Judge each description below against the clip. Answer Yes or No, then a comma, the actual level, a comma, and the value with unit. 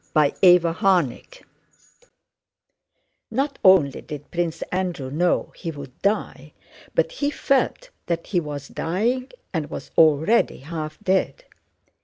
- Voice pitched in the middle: Yes, medium, 175 Hz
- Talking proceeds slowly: Yes, slow, 115 wpm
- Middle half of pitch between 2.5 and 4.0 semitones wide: No, average, 5.2 semitones